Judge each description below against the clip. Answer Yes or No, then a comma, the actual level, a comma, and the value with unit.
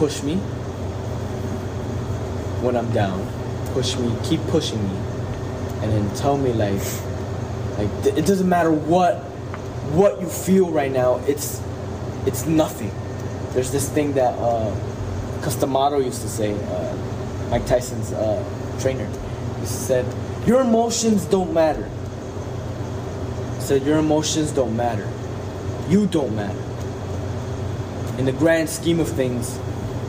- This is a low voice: Yes, low, 125 Hz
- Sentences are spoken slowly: Yes, slow, 130 wpm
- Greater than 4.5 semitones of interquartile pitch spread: No, average, 4.2 semitones